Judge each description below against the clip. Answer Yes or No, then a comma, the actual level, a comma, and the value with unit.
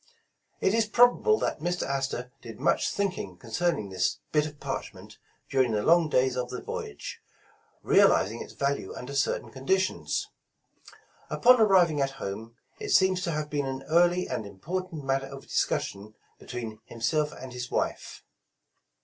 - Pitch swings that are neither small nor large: No, wide, 6.3 semitones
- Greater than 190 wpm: No, average, 160 wpm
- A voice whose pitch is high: No, medium, 140 Hz